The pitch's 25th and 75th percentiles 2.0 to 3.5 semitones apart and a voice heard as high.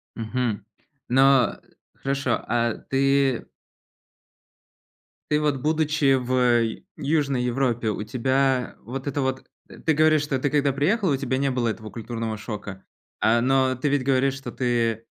No: average, 2.7 semitones; low, 130 Hz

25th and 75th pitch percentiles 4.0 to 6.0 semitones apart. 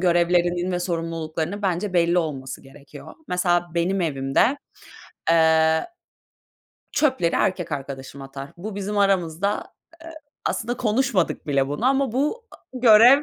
Yes: average, 4.8 semitones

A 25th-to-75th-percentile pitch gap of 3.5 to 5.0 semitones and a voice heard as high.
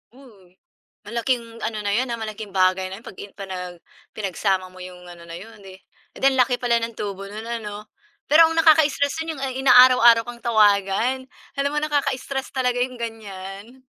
Yes: average, 4.7 semitones; high, 225 Hz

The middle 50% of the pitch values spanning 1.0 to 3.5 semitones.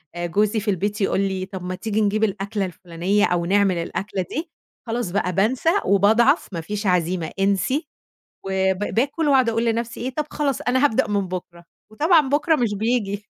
No: average, 4.1 semitones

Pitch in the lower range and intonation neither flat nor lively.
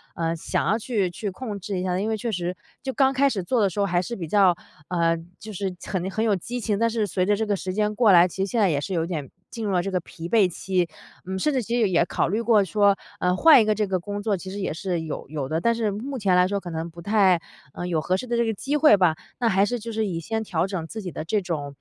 No: high, 195 Hz; average, 3.8 semitones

